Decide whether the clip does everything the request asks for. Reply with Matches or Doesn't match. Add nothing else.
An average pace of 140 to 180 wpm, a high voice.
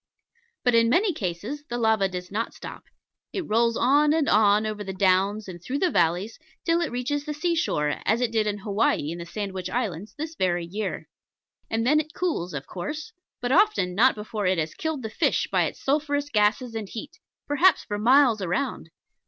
Doesn't match